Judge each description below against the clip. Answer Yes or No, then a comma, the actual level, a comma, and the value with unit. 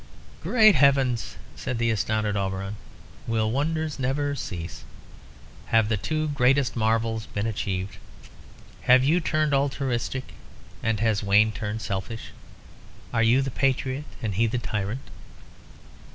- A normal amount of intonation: Yes, average, 4.1 semitones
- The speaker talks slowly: Yes, slow, 125 wpm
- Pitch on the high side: No, low, 115 Hz